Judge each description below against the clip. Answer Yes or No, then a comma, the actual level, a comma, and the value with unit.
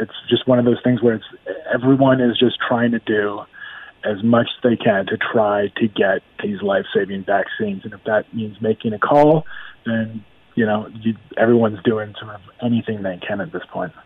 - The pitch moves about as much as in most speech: No, narrow, 2.2 semitones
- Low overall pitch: Yes, low, 115 Hz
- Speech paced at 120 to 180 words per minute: No, fast, 205 wpm